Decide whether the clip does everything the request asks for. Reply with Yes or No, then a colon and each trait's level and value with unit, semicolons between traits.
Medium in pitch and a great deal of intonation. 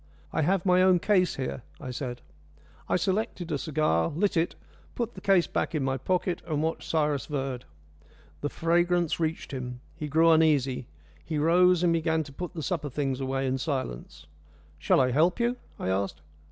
No: medium, 155 Hz; average, 4.7 semitones